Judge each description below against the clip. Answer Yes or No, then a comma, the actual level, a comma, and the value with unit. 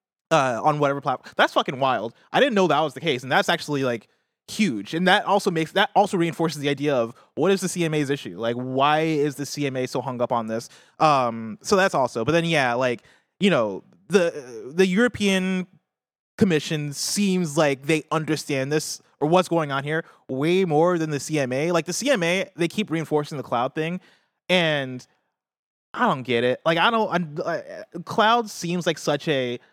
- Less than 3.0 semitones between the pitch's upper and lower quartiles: No, average, 4.7 semitones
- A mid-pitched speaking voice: Yes, medium, 160 Hz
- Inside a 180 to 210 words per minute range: Yes, average, 195 wpm